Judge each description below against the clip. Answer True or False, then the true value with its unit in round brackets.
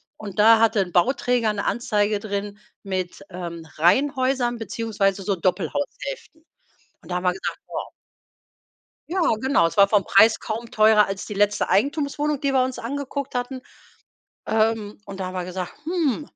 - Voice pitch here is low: False (215 Hz)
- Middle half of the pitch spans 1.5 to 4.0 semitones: False (4.9 semitones)